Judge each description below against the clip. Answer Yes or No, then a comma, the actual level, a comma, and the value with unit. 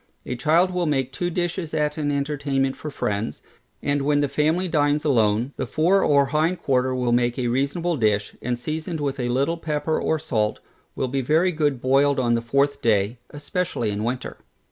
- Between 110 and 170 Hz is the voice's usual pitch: Yes, medium, 140 Hz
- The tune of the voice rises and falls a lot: No, average, 3.9 semitones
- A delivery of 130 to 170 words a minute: No, average, 190 wpm